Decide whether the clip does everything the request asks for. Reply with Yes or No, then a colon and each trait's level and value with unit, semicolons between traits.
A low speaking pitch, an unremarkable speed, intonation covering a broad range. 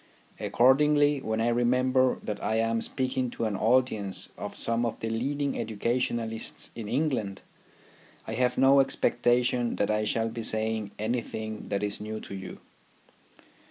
No: low, 115 Hz; average, 150 wpm; average, 2.7 semitones